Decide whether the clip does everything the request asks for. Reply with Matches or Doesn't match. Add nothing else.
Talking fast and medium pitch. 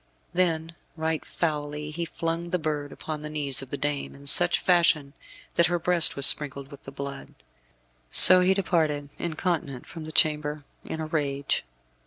Doesn't match